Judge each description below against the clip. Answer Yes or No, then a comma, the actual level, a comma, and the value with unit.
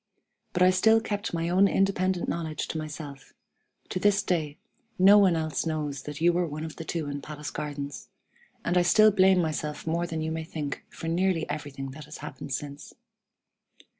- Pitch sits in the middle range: Yes, medium, 160 Hz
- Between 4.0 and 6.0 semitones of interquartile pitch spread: No, average, 3.4 semitones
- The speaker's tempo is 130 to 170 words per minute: No, average, 190 wpm